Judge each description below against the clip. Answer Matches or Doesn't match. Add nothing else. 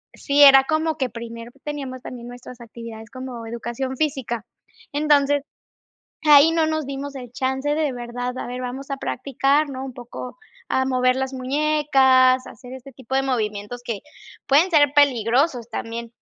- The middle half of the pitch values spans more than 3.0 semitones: Doesn't match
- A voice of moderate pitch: Doesn't match